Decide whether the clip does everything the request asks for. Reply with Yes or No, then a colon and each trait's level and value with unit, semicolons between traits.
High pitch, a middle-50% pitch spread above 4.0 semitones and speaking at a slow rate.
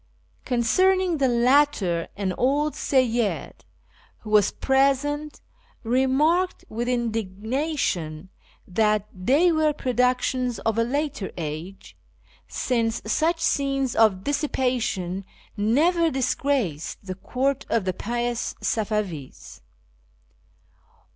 Yes: high, 245 Hz; average, 5.1 semitones; slow, 95 wpm